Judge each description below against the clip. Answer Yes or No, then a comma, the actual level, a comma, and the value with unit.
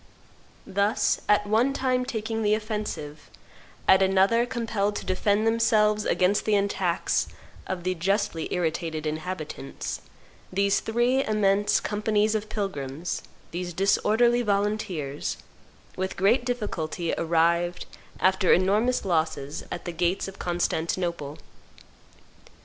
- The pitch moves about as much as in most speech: Yes, average, 3.7 semitones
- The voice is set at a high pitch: Yes, high, 195 Hz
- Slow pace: Yes, slow, 110 wpm